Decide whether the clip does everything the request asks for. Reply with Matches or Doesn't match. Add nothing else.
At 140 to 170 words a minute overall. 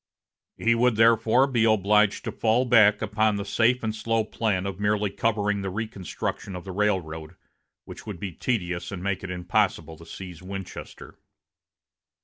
Matches